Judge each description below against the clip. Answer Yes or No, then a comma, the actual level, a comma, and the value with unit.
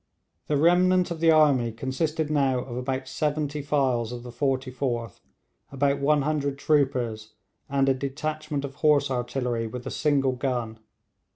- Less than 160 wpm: Yes, average, 145 wpm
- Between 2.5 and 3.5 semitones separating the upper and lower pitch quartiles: Yes, average, 3.2 semitones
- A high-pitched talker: No, low, 135 Hz